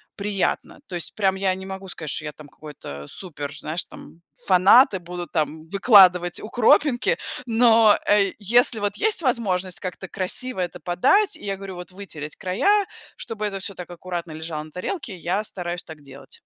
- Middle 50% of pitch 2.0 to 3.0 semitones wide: No, average, 3.4 semitones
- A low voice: No, medium, 185 Hz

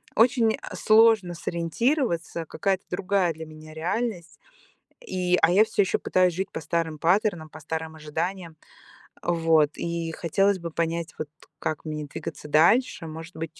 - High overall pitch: No, medium, 170 Hz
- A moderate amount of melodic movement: Yes, average, 3.3 semitones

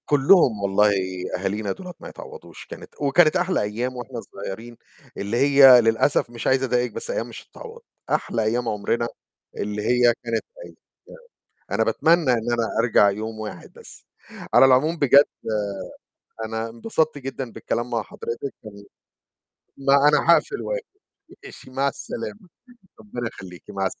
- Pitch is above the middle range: No, low, 120 Hz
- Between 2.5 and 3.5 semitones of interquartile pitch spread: No, average, 4.4 semitones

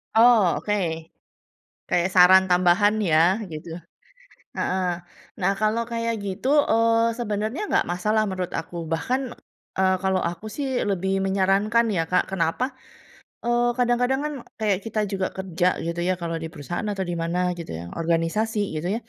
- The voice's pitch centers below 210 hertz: Yes, high, 190 Hz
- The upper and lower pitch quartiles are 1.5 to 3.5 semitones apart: No, average, 4.1 semitones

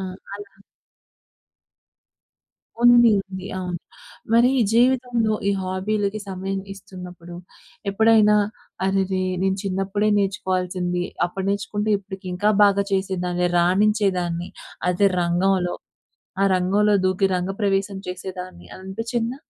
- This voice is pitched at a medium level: No, high, 195 Hz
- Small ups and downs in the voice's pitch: Yes, narrow, 2.3 semitones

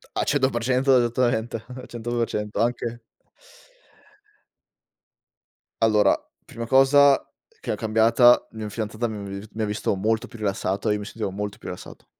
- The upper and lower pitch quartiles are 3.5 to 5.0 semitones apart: No, narrow, 2.5 semitones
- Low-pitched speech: Yes, low, 115 Hz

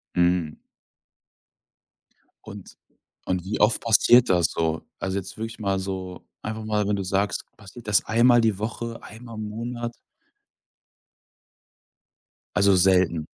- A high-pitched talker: No, low, 100 Hz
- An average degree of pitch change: Yes, average, 3.3 semitones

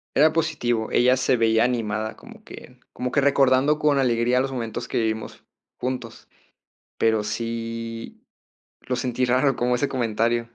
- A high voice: No, low, 120 Hz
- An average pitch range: No, narrow, 2.1 semitones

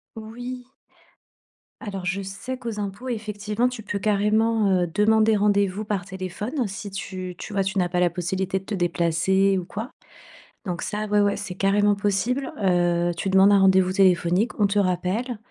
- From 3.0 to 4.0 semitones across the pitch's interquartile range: No, narrow, 2.4 semitones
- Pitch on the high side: Yes, high, 200 Hz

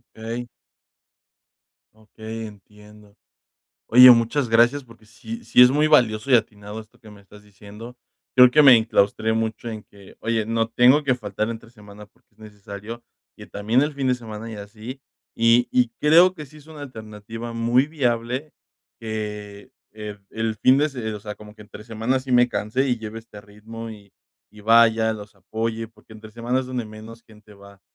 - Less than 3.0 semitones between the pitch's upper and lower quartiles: Yes, narrow, 2.6 semitones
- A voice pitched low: Yes, low, 115 Hz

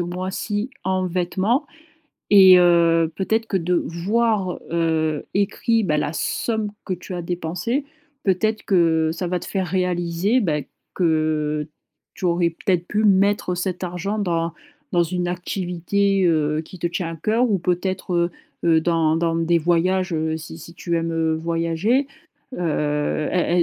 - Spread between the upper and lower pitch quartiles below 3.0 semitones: Yes, narrow, 2.5 semitones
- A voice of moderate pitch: Yes, medium, 175 Hz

